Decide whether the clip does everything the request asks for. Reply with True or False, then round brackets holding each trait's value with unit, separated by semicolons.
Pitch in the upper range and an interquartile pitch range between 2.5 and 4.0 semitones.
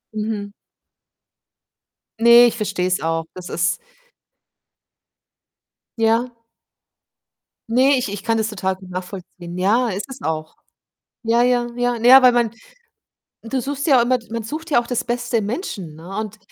False (225 Hz; 4.4 semitones)